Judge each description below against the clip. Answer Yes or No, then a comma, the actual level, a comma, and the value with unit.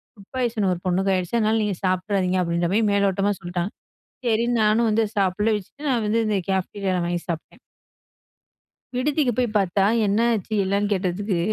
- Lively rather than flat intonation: No, average, 3.1 semitones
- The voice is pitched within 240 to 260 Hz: No, high, 200 Hz